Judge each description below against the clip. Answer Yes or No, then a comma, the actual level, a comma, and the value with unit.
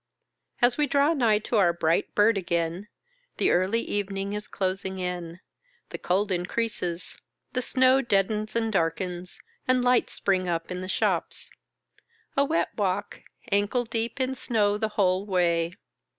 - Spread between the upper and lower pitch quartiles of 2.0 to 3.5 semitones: No, average, 4.2 semitones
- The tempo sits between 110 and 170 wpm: Yes, average, 150 wpm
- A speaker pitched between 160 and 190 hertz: No, high, 200 Hz